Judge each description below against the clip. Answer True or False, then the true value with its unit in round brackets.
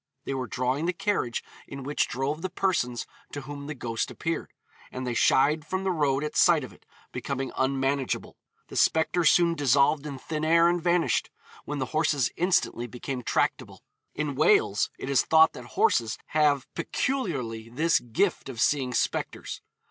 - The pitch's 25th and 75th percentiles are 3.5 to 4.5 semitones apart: True (4.0 semitones)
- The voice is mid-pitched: True (145 Hz)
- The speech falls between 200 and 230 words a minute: False (170 wpm)